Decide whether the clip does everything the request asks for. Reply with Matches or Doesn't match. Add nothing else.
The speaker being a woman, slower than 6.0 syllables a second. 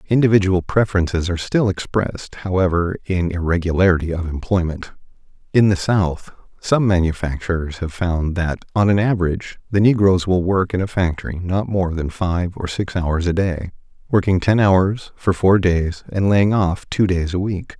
Doesn't match